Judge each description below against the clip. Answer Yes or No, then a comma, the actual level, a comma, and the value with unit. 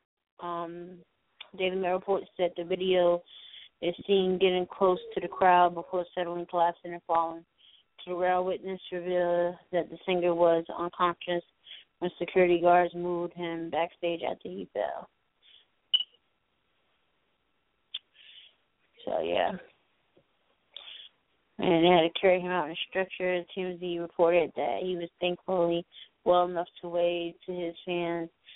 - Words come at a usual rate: No, slow, 130 wpm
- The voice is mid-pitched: Yes, medium, 175 Hz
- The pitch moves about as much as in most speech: No, narrow, 1.0 semitones